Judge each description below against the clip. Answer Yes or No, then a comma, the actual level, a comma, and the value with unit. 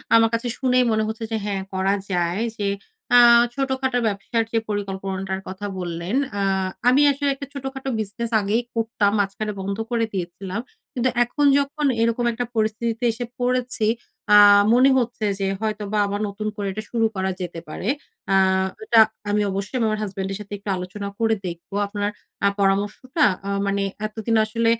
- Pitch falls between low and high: No, high, 215 Hz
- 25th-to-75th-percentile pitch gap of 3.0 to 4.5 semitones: Yes, average, 3.3 semitones